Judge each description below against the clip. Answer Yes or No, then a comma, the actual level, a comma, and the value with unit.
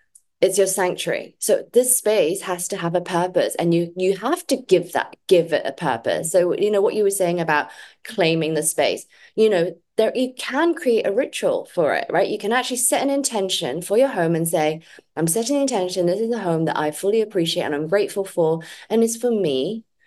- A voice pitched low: No, high, 195 Hz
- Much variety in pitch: Yes, wide, 5.8 semitones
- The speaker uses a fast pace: Yes, fast, 225 wpm